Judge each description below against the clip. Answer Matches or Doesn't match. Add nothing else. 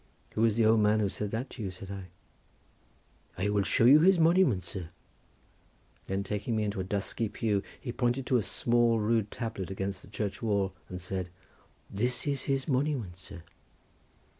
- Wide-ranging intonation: Doesn't match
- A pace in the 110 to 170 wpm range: Doesn't match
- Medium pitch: Doesn't match